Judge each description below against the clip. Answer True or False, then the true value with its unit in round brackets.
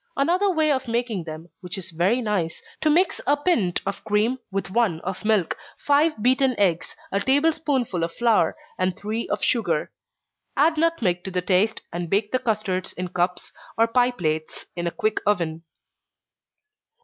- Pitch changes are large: True (6.3 semitones)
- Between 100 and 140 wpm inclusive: False (175 wpm)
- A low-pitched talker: False (210 Hz)